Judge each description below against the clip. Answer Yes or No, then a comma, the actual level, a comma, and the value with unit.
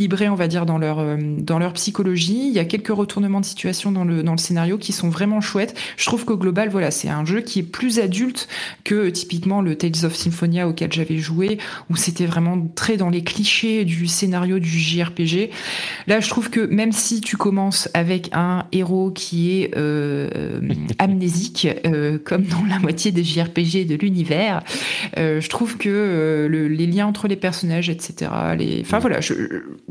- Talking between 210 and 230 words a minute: No, average, 195 wpm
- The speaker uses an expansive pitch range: No, average, 3.3 semitones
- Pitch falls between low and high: Yes, medium, 180 Hz